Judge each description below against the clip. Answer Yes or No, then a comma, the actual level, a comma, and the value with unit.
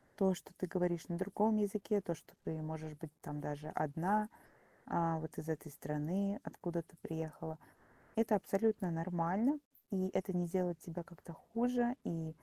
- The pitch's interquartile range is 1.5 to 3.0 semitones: No, average, 3.7 semitones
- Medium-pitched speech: Yes, medium, 175 Hz